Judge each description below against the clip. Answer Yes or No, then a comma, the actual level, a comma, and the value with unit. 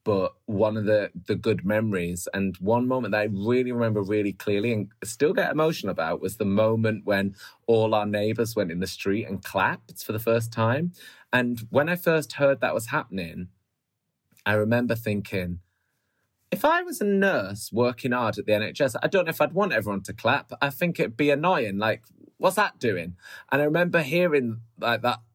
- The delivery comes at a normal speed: Yes, average, 195 wpm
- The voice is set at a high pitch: No, low, 110 Hz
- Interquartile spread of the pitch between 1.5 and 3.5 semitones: No, average, 5.0 semitones